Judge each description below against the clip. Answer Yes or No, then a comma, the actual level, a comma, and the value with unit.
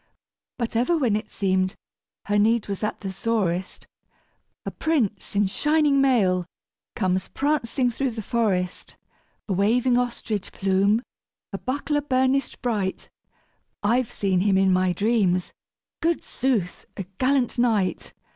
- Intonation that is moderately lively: Yes, average, 4.9 semitones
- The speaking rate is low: Yes, slow, 130 wpm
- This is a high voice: Yes, high, 220 Hz